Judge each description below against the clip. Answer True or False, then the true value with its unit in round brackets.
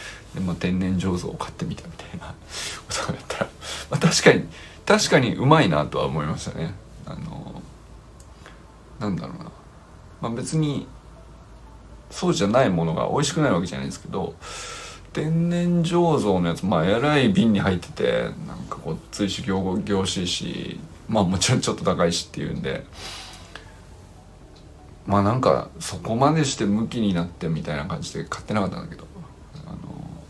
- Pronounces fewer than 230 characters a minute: False (325 characters per minute)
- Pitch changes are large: False (4.2 semitones)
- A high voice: False (95 Hz)